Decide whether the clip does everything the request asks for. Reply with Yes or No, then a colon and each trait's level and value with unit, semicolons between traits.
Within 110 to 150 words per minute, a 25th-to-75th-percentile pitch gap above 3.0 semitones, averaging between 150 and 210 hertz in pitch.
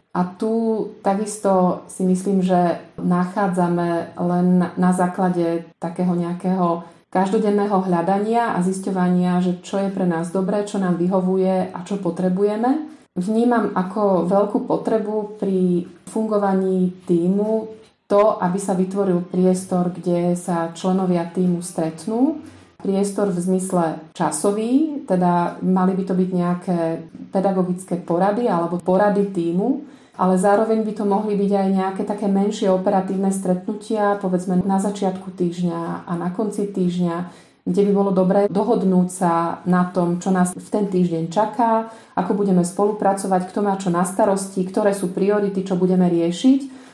No: average, 140 wpm; narrow, 2.4 semitones; high, 190 Hz